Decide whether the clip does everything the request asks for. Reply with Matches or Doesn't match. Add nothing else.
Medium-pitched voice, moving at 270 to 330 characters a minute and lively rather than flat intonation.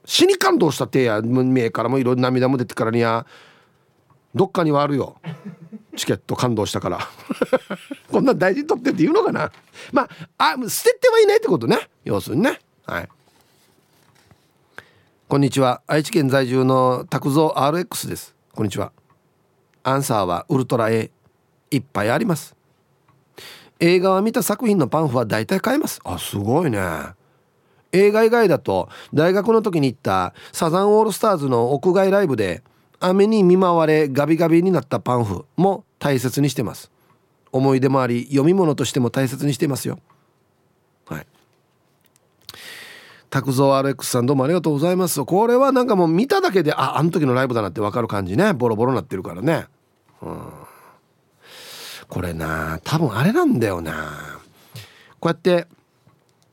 Matches